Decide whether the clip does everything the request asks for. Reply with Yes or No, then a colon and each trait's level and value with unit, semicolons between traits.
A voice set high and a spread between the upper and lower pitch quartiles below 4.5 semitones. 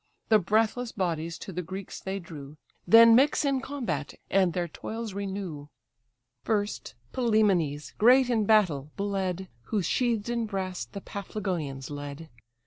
No: high, 195 Hz; average, 4.9 semitones